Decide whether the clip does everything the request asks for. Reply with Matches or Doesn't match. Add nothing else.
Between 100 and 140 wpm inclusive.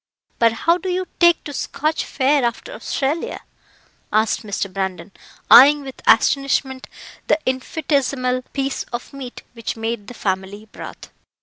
Matches